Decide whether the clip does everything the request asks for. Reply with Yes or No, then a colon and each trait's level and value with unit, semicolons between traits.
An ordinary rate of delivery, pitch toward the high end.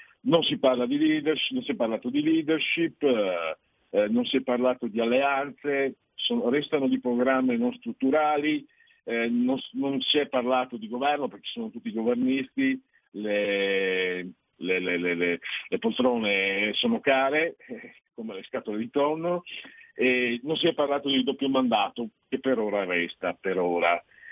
No: average, 150 wpm; low, 135 Hz